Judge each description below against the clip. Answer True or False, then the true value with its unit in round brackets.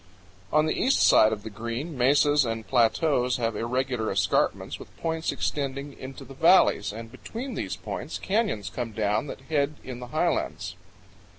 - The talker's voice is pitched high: False (130 Hz)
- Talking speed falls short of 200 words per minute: True (170 wpm)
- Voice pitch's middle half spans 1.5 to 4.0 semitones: False (4.8 semitones)